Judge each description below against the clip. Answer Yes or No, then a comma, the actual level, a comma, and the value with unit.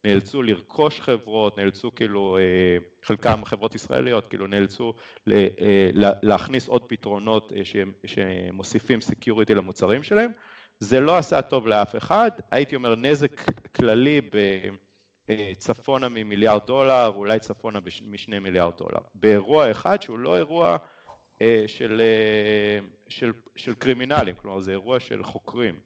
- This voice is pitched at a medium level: No, low, 110 Hz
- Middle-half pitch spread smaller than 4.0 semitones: Yes, average, 3.5 semitones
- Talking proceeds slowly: No, average, 115 wpm